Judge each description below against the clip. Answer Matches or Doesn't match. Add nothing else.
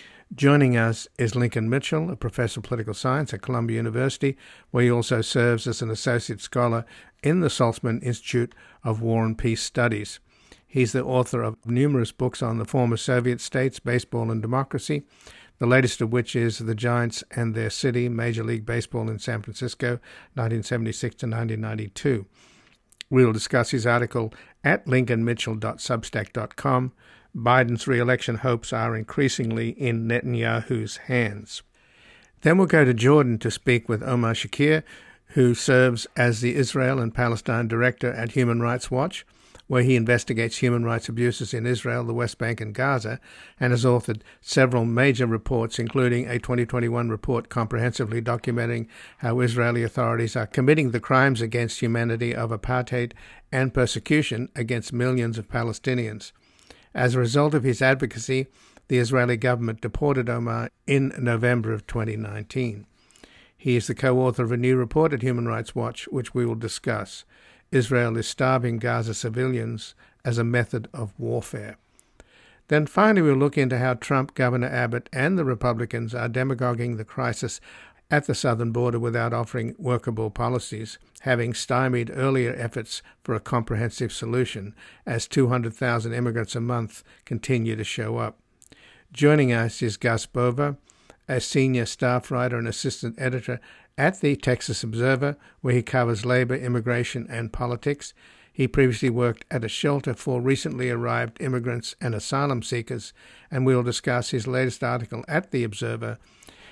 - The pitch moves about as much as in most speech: Doesn't match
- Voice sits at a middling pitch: Doesn't match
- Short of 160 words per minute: Matches